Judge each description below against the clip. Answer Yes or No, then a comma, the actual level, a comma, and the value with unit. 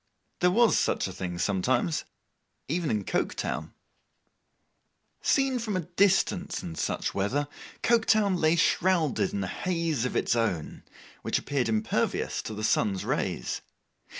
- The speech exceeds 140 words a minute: No, slow, 135 wpm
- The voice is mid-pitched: Yes, medium, 155 Hz